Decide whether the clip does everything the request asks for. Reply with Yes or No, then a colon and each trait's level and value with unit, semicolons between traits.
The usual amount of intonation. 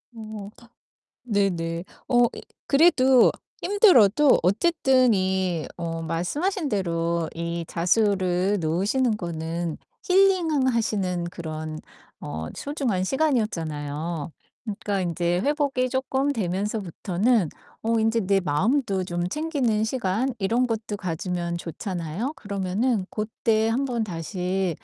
No: wide, 6.4 semitones